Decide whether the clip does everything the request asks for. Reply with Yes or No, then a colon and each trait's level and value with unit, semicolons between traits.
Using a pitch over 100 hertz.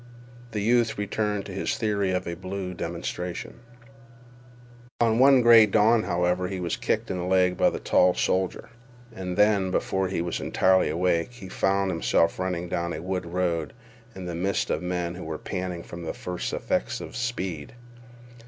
No: very low, 95 Hz